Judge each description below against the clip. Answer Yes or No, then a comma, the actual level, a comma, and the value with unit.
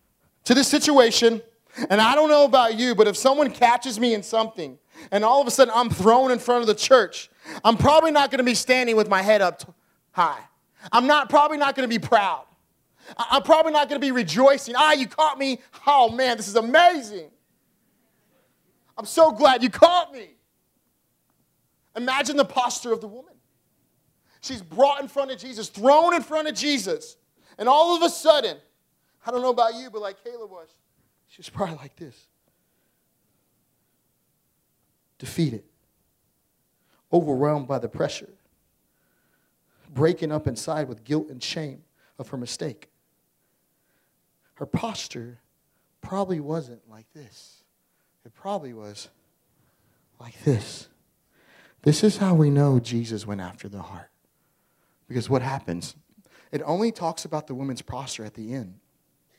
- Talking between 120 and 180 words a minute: Yes, average, 165 wpm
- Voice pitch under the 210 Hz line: No, high, 220 Hz